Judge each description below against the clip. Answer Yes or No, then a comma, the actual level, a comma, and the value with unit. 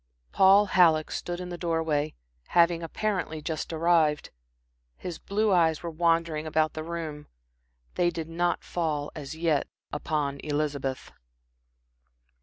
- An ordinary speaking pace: No, slow, 130 wpm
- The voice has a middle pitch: Yes, medium, 165 Hz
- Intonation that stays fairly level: Yes, narrow, 2.2 semitones